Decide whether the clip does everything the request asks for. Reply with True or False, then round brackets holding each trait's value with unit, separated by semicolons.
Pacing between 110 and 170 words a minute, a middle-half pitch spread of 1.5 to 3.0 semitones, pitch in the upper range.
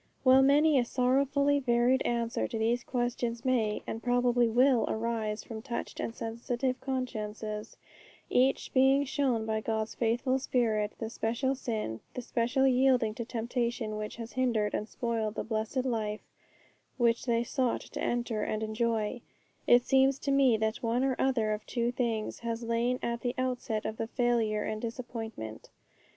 True (160 wpm; 2.5 semitones; 235 Hz)